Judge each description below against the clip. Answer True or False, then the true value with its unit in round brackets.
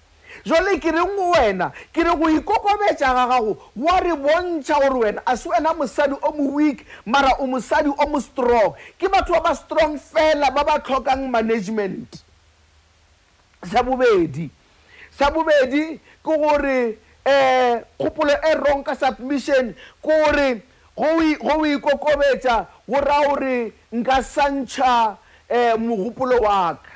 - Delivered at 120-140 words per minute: True (135 wpm)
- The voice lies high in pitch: True (280 Hz)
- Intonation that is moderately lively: True (3.8 semitones)